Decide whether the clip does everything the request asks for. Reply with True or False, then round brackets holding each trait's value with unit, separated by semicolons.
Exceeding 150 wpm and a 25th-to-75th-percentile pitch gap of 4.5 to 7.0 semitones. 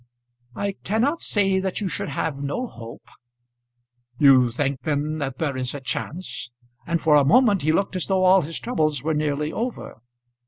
True (180 wpm; 5.4 semitones)